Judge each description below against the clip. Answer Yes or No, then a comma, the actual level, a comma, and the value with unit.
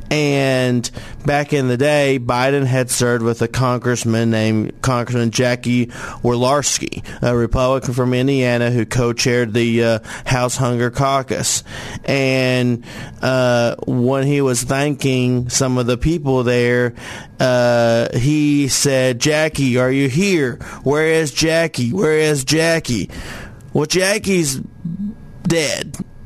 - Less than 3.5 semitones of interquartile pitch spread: Yes, average, 2.7 semitones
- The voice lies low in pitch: Yes, low, 130 Hz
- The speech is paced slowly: Yes, slow, 120 wpm